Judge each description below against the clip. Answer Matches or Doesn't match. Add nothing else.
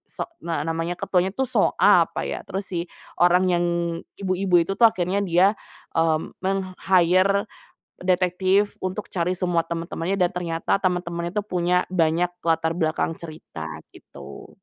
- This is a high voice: Doesn't match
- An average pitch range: Doesn't match